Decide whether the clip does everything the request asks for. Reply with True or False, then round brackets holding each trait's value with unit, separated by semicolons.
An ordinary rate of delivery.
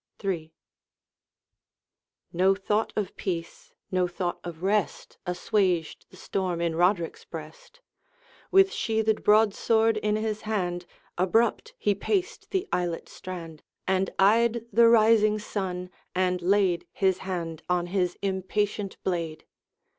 False (120 wpm)